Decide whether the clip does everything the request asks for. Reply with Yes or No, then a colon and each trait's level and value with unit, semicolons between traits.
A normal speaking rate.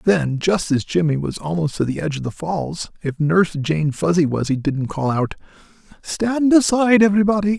Yes: average, 180 wpm